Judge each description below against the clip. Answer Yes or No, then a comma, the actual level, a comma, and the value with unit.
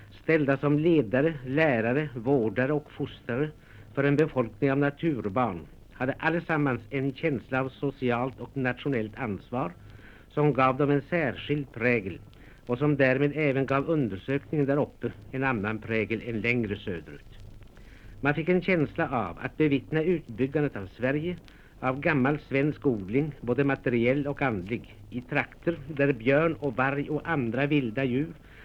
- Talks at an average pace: Yes, average, 145 wpm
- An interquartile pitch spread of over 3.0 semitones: Yes, average, 3.7 semitones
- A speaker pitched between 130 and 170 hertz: Yes, low, 135 Hz